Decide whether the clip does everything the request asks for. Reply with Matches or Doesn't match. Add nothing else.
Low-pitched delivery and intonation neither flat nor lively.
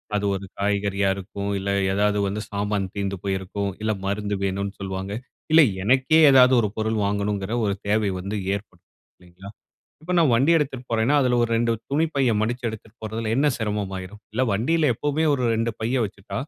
Matches